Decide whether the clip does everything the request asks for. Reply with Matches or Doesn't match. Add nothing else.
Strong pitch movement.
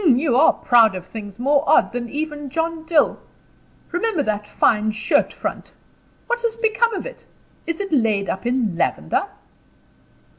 Matches